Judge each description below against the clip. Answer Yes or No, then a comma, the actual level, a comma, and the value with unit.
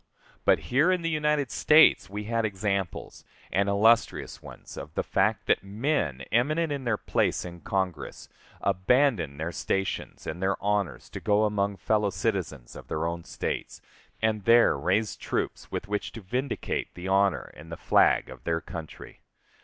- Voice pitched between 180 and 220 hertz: No, low, 100 Hz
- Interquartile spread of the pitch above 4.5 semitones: Yes, average, 4.9 semitones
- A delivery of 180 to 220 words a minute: No, average, 165 wpm